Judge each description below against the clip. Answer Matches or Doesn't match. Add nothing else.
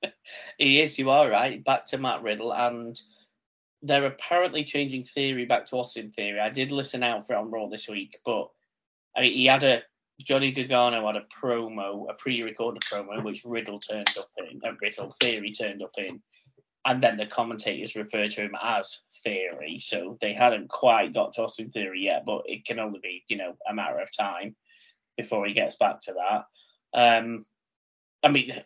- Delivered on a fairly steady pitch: Doesn't match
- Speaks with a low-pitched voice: Matches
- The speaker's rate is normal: Matches